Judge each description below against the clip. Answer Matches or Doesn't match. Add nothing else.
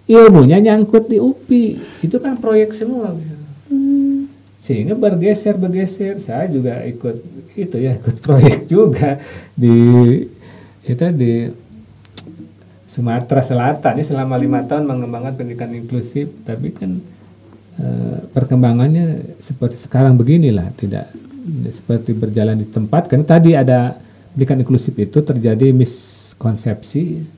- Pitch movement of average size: Doesn't match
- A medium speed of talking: Matches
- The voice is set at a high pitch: Doesn't match